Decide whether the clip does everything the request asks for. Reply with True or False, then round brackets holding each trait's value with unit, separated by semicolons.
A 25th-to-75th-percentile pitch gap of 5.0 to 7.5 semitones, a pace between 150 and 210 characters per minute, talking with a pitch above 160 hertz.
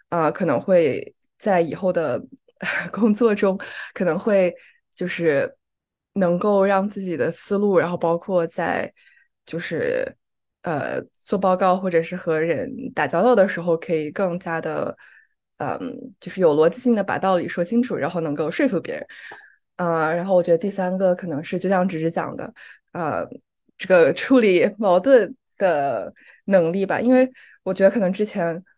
False (5.3 semitones; 235 characters per minute; 190 Hz)